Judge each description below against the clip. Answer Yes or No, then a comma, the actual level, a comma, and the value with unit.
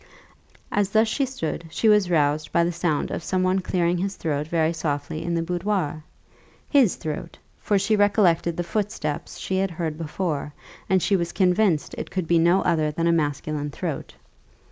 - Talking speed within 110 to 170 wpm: No, average, 185 wpm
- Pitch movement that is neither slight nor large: Yes, average, 3.5 semitones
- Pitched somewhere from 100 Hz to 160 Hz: No, medium, 170 Hz